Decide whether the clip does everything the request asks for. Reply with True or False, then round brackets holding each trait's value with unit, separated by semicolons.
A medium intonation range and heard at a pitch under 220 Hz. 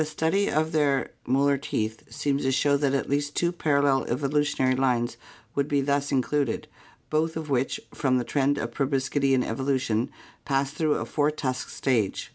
False (1.9 semitones; 140 Hz)